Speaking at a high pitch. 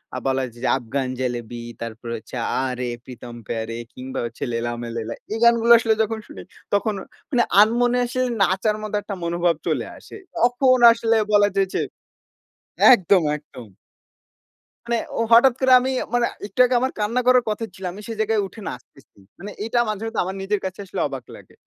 Yes: high, 200 Hz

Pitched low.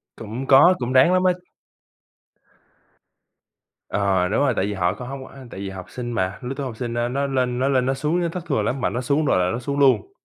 Yes: low, 125 Hz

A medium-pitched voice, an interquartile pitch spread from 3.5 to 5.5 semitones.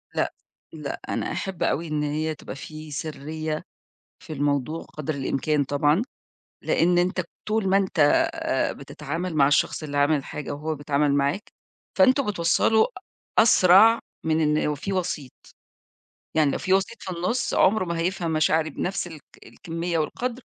Yes: medium, 160 Hz; average, 3.8 semitones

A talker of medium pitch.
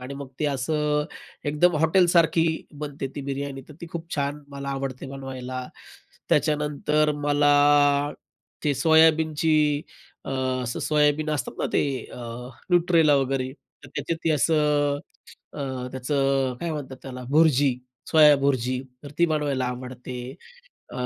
Yes: medium, 145 Hz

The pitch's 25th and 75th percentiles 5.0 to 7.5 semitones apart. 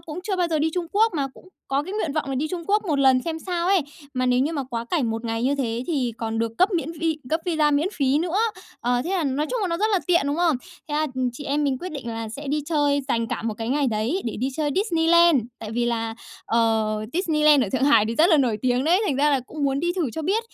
Yes: average, 5.3 semitones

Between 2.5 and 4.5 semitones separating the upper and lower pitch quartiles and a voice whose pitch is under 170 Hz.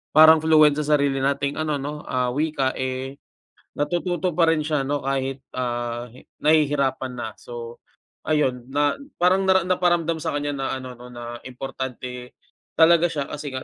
Yes: average, 3.4 semitones; medium, 140 Hz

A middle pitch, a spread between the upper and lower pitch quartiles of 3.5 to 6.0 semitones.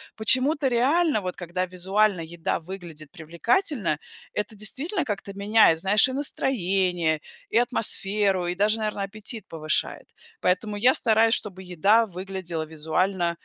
No: high, 200 Hz; average, 4.2 semitones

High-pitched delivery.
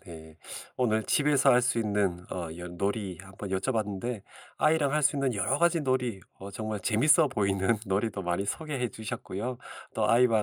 No: low, 110 Hz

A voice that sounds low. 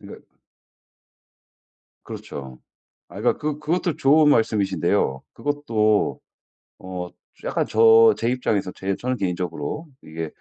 Yes: low, 110 Hz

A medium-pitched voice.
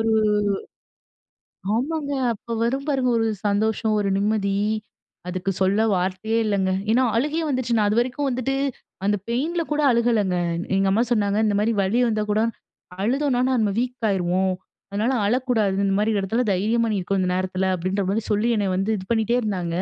No: high, 215 Hz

